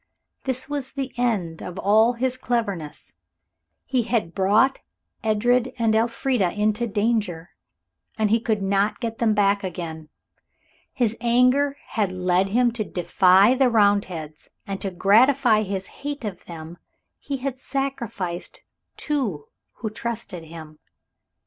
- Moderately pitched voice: No, high, 215 Hz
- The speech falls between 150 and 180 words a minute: No, slow, 135 wpm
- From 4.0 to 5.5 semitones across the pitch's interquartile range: Yes, average, 4.7 semitones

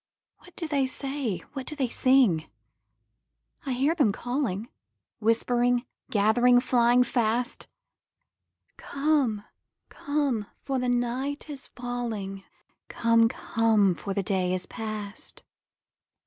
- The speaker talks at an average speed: No, slow, 110 wpm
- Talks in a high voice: Yes, high, 245 Hz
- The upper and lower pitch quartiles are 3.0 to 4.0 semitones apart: Yes, average, 3.7 semitones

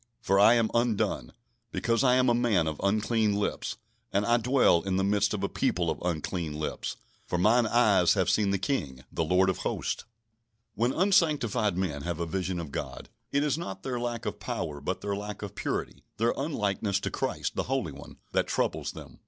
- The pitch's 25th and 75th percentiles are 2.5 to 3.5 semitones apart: No, average, 4.7 semitones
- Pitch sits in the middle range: No, low, 100 Hz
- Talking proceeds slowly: No, average, 200 wpm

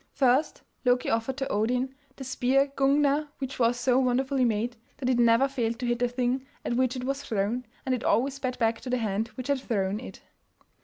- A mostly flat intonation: Yes, narrow, 2.2 semitones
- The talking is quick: Yes, fast, 210 wpm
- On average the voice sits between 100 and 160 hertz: No, very high, 250 Hz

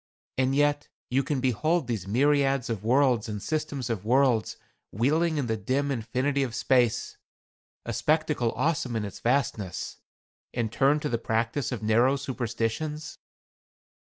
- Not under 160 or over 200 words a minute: No, average, 145 wpm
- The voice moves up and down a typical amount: Yes, average, 3.9 semitones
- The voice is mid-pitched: No, low, 130 Hz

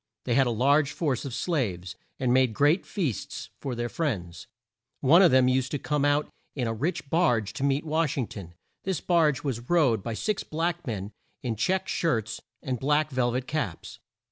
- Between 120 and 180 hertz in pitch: Yes, low, 135 Hz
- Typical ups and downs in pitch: Yes, average, 4.7 semitones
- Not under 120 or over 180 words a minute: No, average, 195 wpm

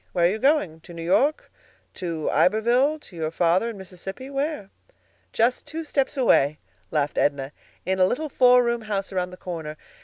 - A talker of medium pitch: No, high, 195 Hz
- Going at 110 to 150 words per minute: No, average, 180 wpm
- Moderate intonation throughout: No, wide, 6.7 semitones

